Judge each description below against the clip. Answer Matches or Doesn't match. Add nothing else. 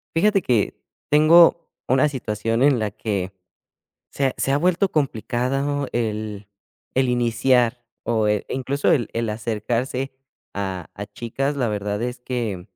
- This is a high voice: Doesn't match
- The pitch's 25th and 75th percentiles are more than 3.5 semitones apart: Matches